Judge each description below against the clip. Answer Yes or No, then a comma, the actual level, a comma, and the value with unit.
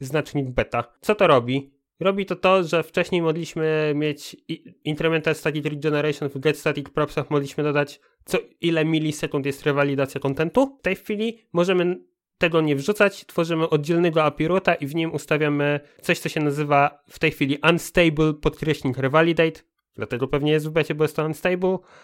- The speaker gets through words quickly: Yes, fast, 165 wpm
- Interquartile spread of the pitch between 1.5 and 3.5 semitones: Yes, average, 2.8 semitones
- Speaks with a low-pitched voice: No, medium, 155 Hz